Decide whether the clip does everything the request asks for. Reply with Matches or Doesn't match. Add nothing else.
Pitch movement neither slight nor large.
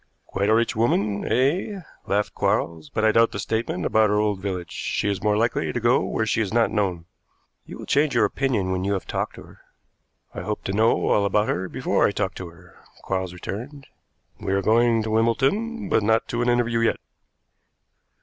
Matches